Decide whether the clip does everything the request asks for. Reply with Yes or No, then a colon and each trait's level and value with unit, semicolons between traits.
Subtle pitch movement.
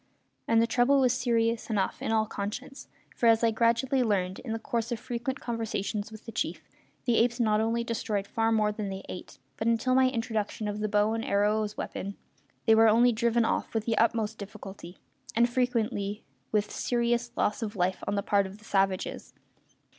Yes: narrow, 2.2 semitones